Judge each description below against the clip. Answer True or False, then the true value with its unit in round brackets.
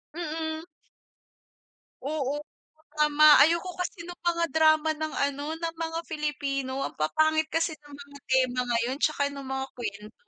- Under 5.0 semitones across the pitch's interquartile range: True (2.7 semitones)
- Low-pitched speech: False (300 Hz)